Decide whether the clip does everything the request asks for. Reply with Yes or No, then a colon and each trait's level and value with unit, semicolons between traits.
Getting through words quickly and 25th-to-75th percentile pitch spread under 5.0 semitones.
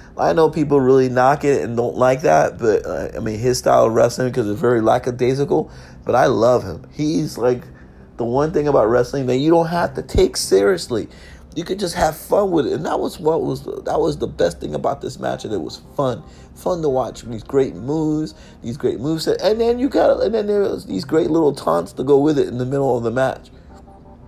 No: fast, 235 wpm; wide, 5.5 semitones